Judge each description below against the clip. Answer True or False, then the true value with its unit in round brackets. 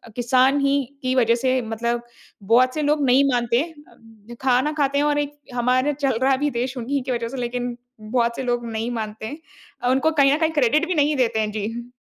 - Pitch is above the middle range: True (255 Hz)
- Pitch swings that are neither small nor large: True (3.1 semitones)